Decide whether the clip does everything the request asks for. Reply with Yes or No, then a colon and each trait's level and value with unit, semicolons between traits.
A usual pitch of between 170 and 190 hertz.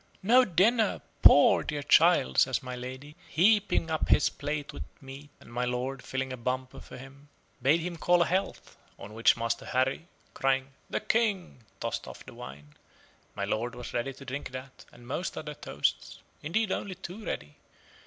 No: low, 135 Hz